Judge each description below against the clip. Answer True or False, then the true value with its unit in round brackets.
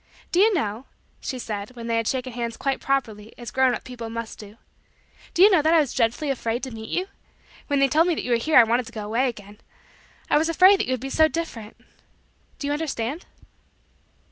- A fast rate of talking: True (230 wpm)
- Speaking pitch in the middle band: False (255 Hz)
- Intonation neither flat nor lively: True (4.8 semitones)